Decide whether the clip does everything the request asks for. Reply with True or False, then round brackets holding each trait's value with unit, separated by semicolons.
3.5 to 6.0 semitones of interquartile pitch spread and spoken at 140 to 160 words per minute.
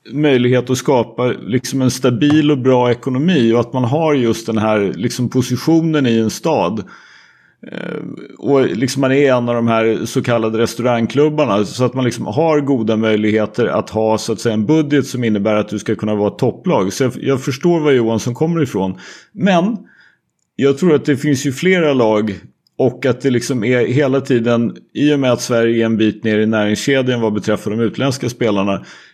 False (3.8 semitones; 190 wpm)